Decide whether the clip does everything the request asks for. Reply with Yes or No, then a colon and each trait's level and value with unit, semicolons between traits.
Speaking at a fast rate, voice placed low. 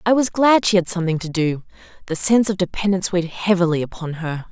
No: fast, 215 wpm; medium, 185 Hz